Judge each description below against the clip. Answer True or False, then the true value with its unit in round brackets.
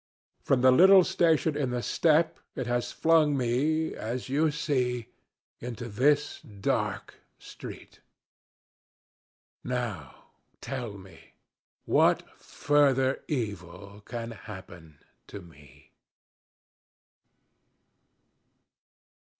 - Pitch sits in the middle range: False (125 Hz)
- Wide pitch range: True (5.7 semitones)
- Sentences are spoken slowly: True (85 wpm)